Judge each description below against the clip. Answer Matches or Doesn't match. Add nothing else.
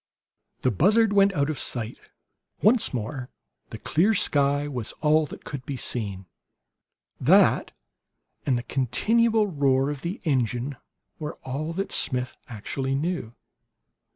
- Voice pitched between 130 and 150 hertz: Matches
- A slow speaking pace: Matches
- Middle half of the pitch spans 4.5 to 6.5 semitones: Matches